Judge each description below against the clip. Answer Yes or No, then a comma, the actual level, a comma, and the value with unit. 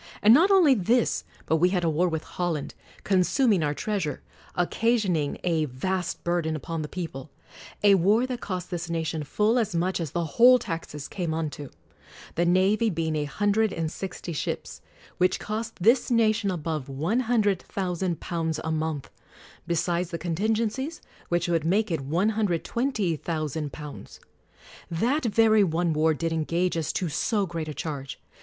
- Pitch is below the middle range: No, medium, 175 Hz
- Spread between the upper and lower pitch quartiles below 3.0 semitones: No, average, 4.8 semitones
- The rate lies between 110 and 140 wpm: No, average, 155 wpm